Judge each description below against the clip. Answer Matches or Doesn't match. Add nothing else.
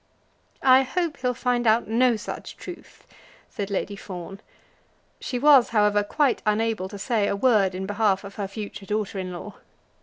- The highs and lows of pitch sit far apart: Doesn't match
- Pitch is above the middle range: Matches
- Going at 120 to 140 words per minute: Doesn't match